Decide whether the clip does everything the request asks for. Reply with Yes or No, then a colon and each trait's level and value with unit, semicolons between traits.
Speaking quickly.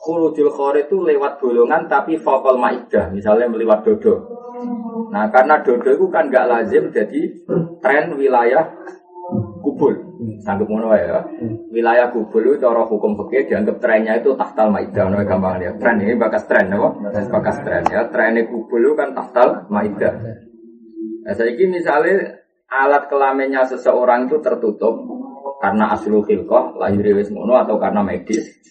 Yes: fast, 145 wpm